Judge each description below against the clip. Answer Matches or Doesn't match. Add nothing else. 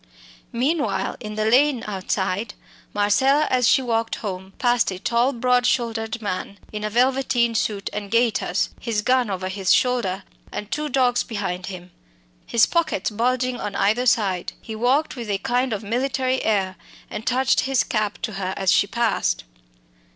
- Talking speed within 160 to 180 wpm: Matches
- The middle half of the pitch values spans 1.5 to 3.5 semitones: Doesn't match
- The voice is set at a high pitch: Matches